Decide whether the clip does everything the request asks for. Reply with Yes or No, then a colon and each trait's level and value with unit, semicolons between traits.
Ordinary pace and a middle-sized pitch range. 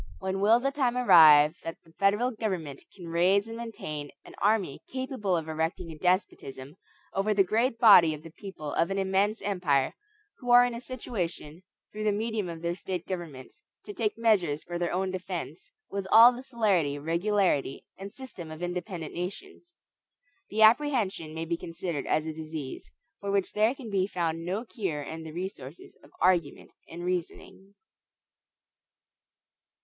Yes: average, 165 wpm; average, 4.7 semitones